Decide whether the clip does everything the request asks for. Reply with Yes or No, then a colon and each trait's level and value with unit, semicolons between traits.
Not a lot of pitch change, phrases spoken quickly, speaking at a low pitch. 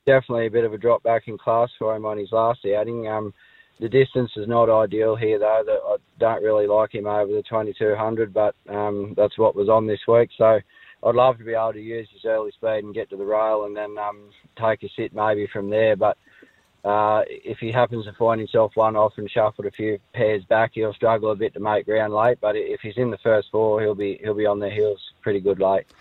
Yes: narrow, 1.5 semitones; fast, 245 wpm; low, 110 Hz